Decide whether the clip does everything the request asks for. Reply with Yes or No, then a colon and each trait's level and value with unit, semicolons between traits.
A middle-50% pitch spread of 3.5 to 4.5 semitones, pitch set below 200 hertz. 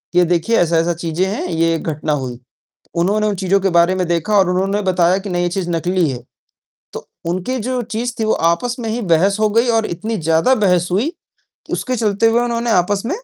Yes: average, 4.2 semitones; medium, 185 Hz